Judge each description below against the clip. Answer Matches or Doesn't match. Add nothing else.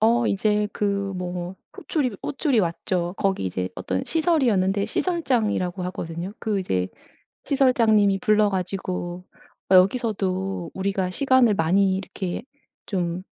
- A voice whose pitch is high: Matches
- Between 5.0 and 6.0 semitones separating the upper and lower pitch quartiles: Doesn't match